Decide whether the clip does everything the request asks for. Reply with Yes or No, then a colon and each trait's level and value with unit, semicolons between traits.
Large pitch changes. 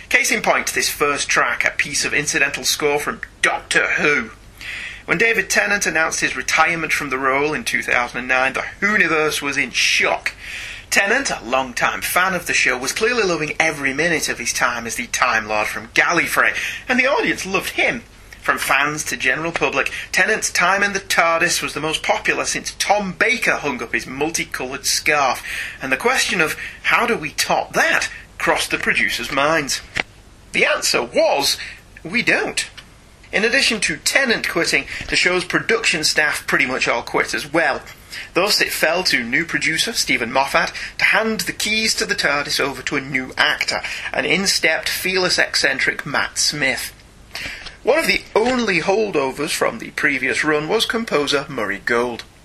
Yes: wide, 5.8 semitones